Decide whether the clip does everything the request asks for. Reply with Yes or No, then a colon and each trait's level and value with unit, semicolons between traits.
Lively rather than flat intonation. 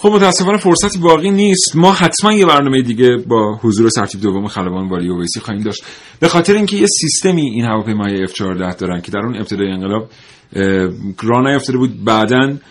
Yes: wide, 8.6 semitones